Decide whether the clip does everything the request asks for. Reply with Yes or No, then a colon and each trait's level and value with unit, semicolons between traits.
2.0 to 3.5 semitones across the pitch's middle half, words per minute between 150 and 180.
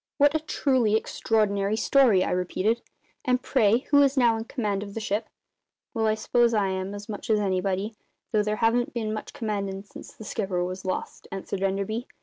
No: average, 2.8 semitones; average, 190 wpm